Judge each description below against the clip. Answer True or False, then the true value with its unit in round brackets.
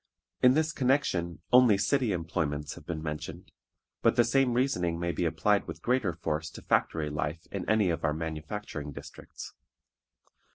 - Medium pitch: False (85 Hz)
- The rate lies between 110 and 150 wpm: False (160 wpm)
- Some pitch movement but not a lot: False (7.1 semitones)